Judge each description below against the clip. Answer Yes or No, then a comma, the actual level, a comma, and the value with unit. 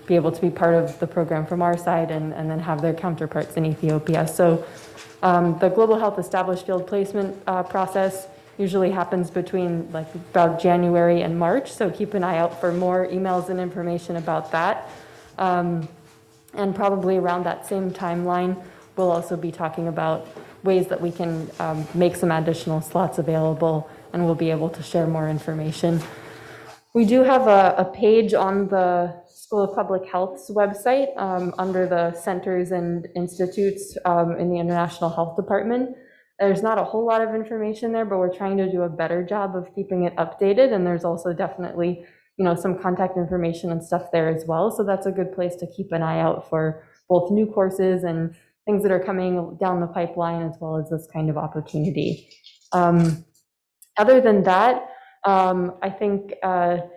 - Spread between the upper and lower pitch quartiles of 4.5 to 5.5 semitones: No, narrow, 2.4 semitones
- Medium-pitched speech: Yes, medium, 180 Hz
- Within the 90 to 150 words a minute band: No, average, 185 wpm